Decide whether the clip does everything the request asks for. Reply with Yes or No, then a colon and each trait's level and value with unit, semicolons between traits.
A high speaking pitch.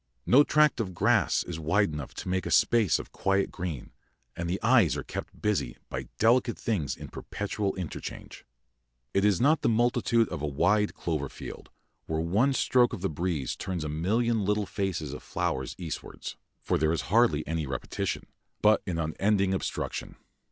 No: very low, 95 Hz